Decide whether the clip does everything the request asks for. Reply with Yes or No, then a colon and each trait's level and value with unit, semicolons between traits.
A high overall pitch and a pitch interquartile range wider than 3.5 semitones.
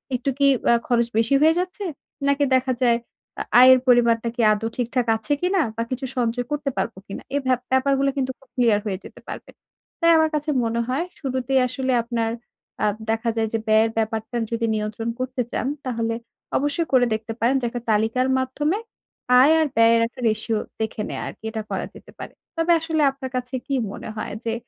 No: high, 245 Hz; average, 3.2 semitones